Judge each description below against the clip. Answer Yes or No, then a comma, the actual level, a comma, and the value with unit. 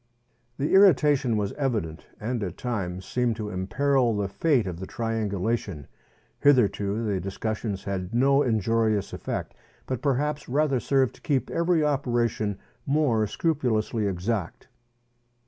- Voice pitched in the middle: No, low, 115 Hz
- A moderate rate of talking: No, slow, 130 wpm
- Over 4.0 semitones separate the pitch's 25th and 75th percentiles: Yes, average, 5.2 semitones